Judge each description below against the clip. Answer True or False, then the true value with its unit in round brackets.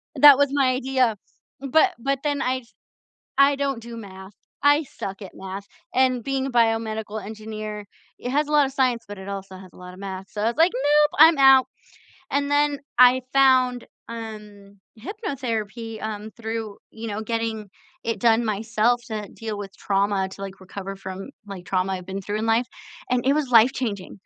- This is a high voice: True (225 Hz)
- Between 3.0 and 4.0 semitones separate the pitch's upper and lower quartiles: False (4.7 semitones)